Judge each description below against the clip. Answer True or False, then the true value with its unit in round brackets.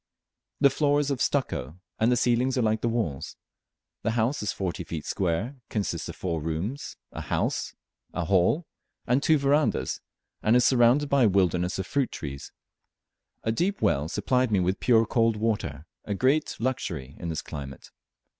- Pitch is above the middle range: False (110 Hz)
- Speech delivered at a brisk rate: False (165 wpm)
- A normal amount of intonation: False (6.7 semitones)